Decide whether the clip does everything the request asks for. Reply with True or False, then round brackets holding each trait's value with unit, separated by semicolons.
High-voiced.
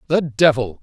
False (135 Hz)